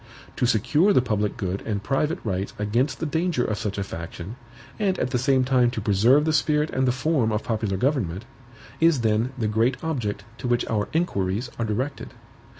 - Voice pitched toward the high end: No, low, 120 Hz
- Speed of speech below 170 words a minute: No, average, 195 wpm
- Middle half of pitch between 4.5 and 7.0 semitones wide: Yes, average, 5.1 semitones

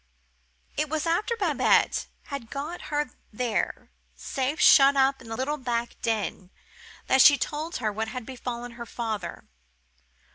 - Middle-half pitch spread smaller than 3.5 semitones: No, average, 4.1 semitones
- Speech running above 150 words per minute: No, average, 145 wpm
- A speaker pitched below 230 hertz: No, very high, 260 Hz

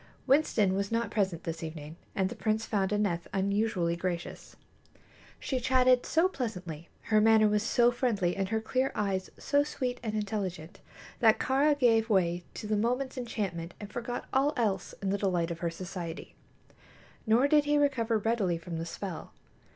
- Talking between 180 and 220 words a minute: No, average, 170 wpm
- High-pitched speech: Yes, high, 210 Hz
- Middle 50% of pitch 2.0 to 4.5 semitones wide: No, average, 5.1 semitones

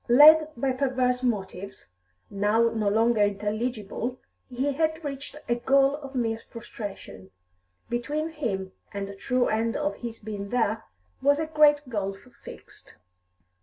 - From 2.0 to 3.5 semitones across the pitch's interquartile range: No, average, 4.7 semitones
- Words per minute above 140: No, slow, 135 wpm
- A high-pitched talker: Yes, high, 240 Hz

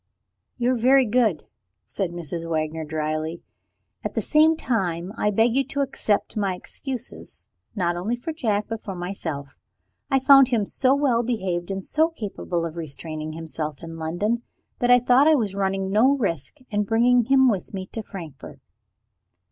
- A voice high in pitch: Yes, high, 205 Hz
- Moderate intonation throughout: No, wide, 6.6 semitones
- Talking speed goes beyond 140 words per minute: Yes, average, 170 wpm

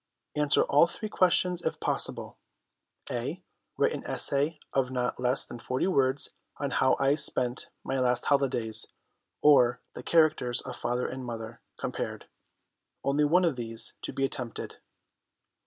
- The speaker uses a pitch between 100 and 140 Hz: Yes, low, 135 Hz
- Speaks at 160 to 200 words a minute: No, average, 145 wpm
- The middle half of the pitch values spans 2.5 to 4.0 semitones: Yes, average, 3.4 semitones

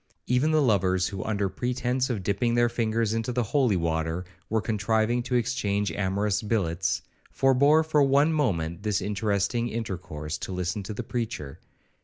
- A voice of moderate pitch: No, low, 110 Hz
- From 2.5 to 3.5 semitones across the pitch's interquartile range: No, average, 4.4 semitones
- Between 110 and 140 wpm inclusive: No, average, 160 wpm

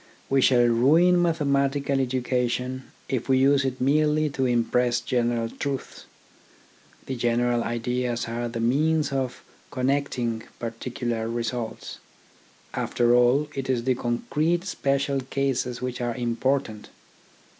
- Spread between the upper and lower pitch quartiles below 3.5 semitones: Yes, narrow, 2.5 semitones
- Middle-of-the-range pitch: No, low, 125 Hz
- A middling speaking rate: No, slow, 120 wpm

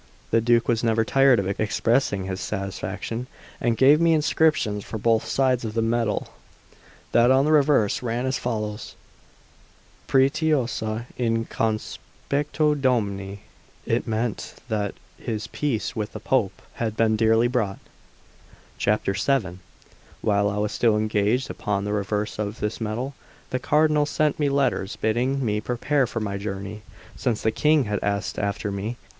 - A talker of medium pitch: No, low, 115 Hz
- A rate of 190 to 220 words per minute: No, average, 150 wpm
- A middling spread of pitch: Yes, average, 4.0 semitones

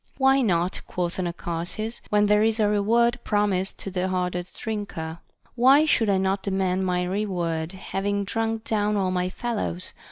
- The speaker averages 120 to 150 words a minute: No, average, 160 wpm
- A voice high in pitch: Yes, high, 195 Hz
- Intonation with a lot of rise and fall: No, average, 3.1 semitones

